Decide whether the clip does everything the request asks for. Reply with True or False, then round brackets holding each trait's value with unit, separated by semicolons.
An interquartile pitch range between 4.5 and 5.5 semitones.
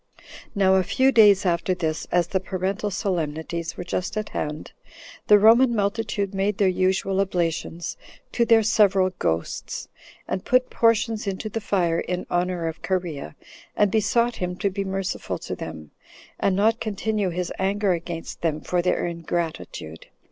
False (3.3 semitones)